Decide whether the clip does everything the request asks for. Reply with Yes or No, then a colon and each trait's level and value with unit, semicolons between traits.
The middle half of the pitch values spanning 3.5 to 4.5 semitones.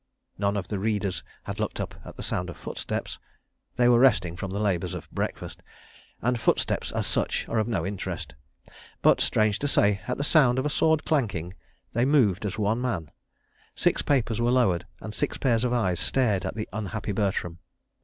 Yes: average, 4.2 semitones